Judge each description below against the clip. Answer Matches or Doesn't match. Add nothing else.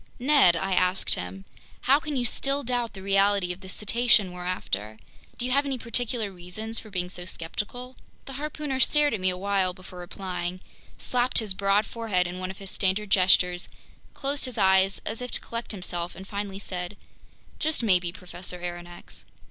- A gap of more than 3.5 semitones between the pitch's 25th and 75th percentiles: Matches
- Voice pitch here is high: Matches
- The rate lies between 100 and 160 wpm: Doesn't match